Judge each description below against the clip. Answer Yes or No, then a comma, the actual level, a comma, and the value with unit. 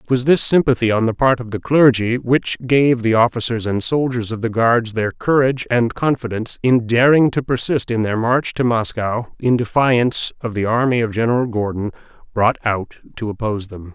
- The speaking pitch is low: Yes, low, 120 Hz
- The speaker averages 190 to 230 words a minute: Yes, average, 195 wpm